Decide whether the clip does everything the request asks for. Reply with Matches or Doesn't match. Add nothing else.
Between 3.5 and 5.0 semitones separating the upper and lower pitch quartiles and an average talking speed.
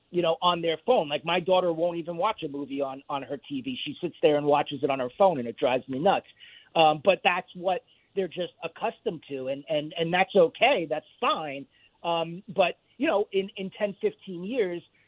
Doesn't match